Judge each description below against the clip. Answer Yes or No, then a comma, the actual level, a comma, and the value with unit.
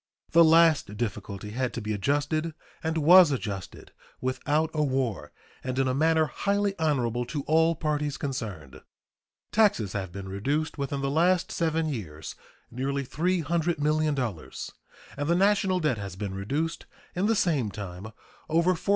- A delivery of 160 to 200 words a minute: No, average, 150 wpm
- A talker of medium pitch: Yes, medium, 145 Hz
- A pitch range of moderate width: No, wide, 6.3 semitones